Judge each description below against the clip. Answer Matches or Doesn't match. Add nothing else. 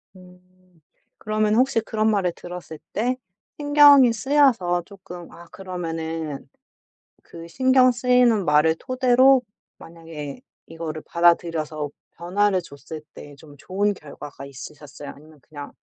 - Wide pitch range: Matches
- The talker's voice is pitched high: Doesn't match